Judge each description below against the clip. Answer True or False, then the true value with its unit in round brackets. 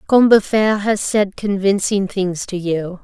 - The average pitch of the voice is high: True (200 Hz)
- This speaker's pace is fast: False (140 wpm)